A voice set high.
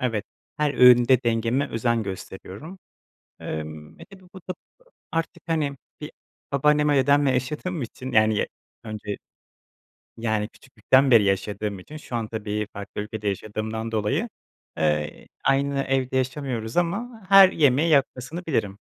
No: low, 125 Hz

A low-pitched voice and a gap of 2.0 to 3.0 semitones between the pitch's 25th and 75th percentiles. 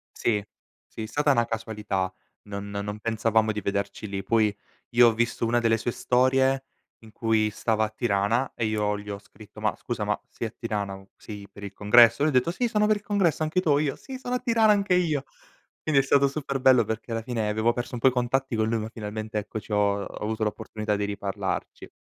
No: low, 115 Hz; average, 4.1 semitones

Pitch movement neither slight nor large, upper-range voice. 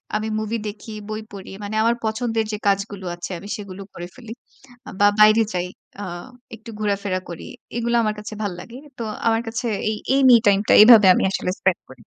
No: narrow, 2.2 semitones; high, 215 Hz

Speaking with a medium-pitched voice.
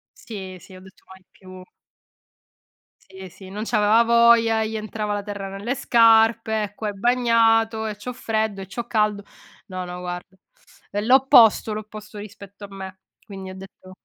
No: high, 210 Hz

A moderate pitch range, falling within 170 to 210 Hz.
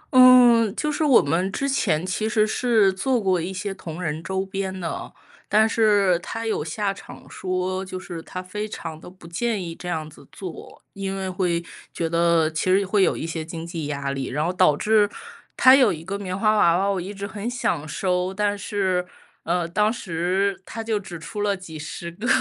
Yes: average, 3.7 semitones; high, 190 Hz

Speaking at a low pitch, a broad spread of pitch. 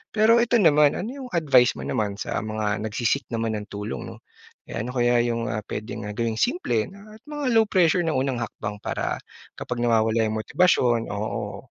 Yes: low, 120 Hz; wide, 8.0 semitones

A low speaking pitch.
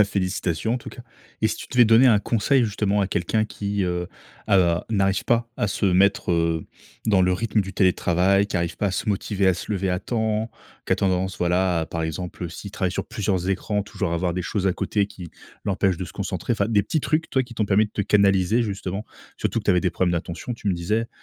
Yes: low, 100 Hz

